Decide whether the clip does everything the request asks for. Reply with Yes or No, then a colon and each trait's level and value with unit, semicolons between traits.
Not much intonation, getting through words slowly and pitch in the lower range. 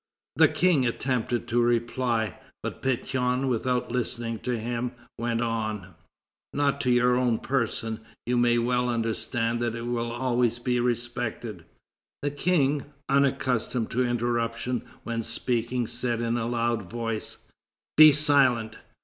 Yes: narrow, 1.5 semitones; slow, 130 wpm; low, 120 Hz